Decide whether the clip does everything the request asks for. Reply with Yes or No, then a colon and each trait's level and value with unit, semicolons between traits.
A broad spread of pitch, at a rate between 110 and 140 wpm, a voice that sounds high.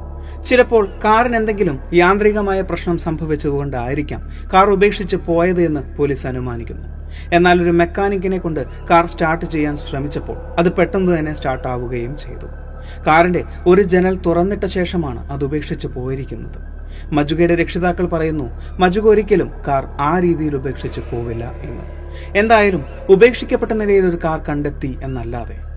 No: wide, 6.5 semitones; average, 120 wpm; medium, 165 Hz